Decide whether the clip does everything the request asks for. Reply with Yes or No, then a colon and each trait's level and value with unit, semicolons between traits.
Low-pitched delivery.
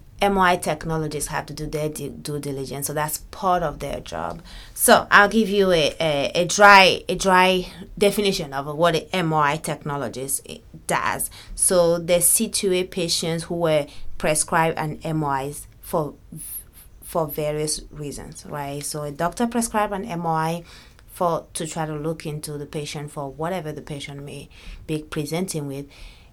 No: medium, 155 Hz